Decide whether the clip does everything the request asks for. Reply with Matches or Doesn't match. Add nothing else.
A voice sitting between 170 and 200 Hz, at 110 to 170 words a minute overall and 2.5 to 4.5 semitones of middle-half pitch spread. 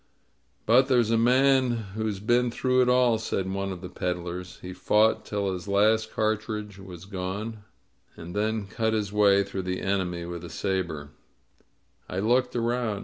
Doesn't match